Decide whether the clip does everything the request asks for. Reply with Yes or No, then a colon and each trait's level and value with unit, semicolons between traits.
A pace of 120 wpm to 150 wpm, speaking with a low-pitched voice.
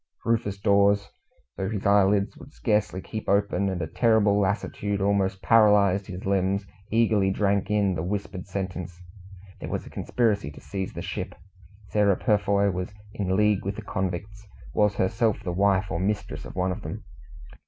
No: average, 165 wpm; low, 100 Hz